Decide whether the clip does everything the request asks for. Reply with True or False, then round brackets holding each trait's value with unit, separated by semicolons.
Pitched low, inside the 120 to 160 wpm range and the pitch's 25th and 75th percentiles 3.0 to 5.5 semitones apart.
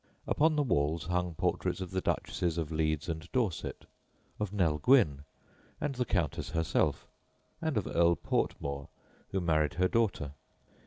True (85 Hz; 150 wpm; 5.2 semitones)